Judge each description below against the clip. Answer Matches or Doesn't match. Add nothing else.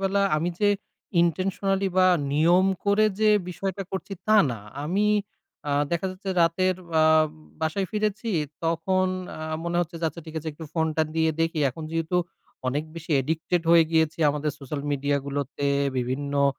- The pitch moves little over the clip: Doesn't match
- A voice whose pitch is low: Doesn't match